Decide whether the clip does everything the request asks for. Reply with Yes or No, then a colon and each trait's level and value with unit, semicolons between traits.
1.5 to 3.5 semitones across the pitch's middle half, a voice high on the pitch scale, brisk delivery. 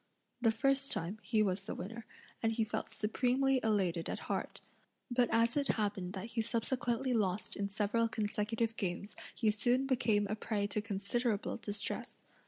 No: average, 2.7 semitones; high, 220 Hz; average, 165 wpm